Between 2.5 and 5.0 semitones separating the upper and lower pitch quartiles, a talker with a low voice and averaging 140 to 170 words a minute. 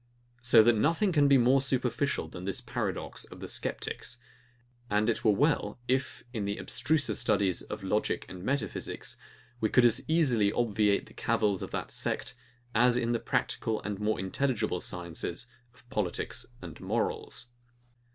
Yes: average, 4.1 semitones; low, 115 Hz; average, 160 wpm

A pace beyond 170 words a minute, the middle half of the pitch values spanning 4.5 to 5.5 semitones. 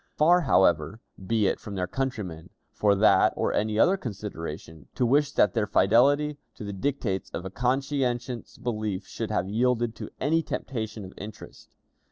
No: average, 165 wpm; average, 5.1 semitones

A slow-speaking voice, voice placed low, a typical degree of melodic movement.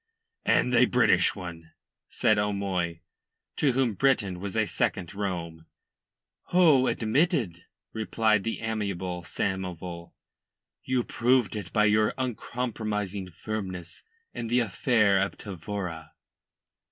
Yes: slow, 110 wpm; low, 105 Hz; average, 3.8 semitones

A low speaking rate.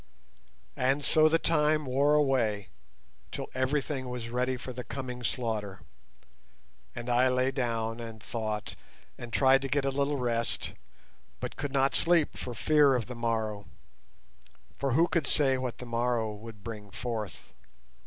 No: average, 150 wpm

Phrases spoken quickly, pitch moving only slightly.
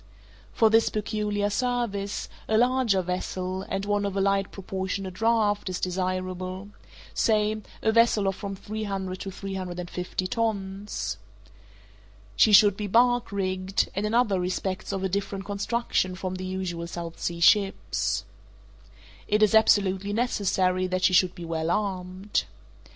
No: average, 150 wpm; narrow, 2.2 semitones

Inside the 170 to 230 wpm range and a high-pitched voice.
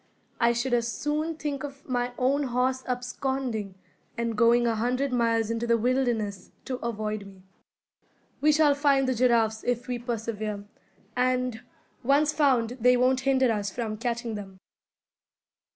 No: average, 150 wpm; high, 245 Hz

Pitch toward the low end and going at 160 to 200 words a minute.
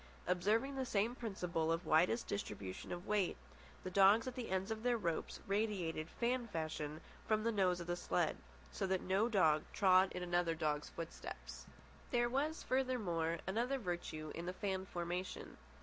No: high, 190 Hz; average, 165 wpm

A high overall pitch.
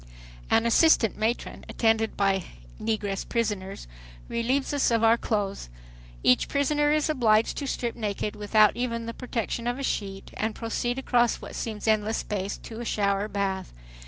Yes: high, 225 Hz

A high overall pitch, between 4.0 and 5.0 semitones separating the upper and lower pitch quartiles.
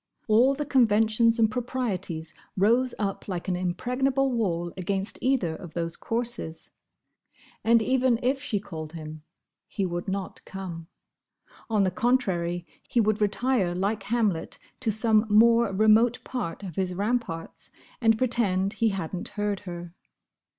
Yes: high, 210 Hz; average, 4.7 semitones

